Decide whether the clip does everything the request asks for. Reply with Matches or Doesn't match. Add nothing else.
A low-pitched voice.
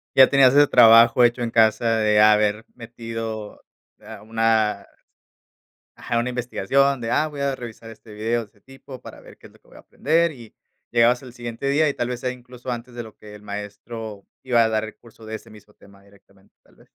Matches